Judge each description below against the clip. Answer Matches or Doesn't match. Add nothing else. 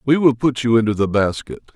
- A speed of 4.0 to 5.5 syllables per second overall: Doesn't match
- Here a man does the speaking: Matches